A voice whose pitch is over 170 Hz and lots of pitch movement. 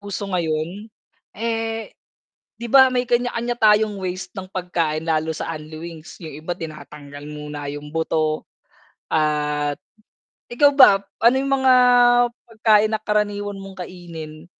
Yes: medium, 185 Hz; wide, 6.1 semitones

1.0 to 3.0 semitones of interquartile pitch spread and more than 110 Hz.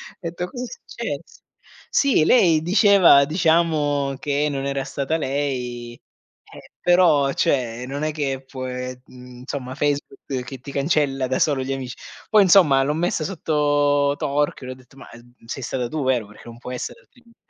No: average, 3.5 semitones; medium, 140 Hz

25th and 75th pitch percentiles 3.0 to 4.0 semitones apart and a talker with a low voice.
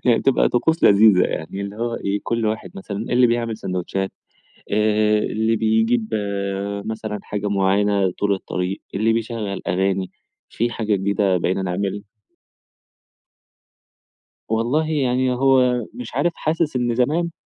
Yes: average, 3.4 semitones; low, 110 Hz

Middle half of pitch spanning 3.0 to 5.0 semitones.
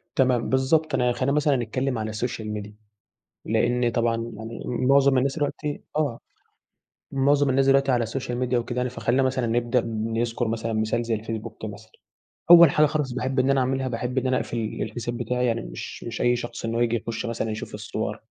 No: narrow, 2.5 semitones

